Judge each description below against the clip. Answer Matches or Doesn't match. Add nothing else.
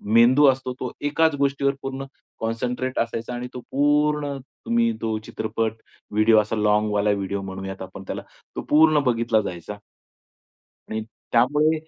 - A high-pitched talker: Doesn't match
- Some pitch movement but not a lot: Matches